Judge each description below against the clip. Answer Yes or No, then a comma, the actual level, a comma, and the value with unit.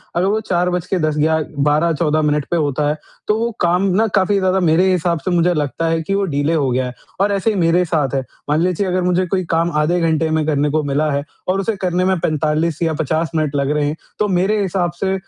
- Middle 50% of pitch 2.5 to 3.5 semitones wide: Yes, average, 3.2 semitones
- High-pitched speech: No, medium, 165 Hz